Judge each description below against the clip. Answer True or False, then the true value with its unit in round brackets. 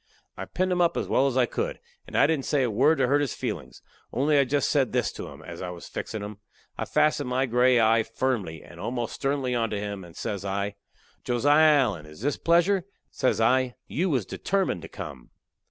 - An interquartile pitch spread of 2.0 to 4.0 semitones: False (5.5 semitones)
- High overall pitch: False (125 Hz)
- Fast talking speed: True (220 wpm)